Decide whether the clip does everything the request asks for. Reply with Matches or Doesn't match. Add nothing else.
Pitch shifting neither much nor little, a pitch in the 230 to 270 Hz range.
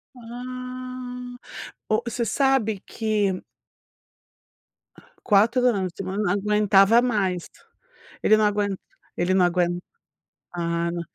Doesn't match